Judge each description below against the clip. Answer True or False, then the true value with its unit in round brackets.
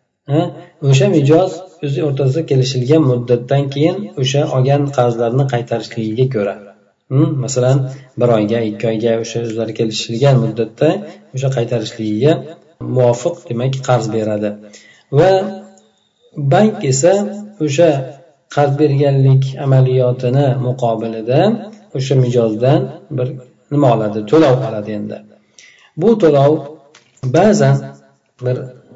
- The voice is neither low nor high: False (130 Hz)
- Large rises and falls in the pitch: False (4.1 semitones)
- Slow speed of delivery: True (95 wpm)